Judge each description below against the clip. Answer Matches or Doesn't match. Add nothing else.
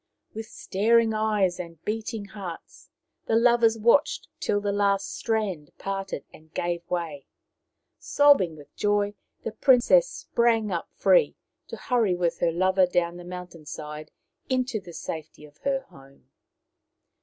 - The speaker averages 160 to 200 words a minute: Doesn't match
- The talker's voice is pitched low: Doesn't match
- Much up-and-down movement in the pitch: Doesn't match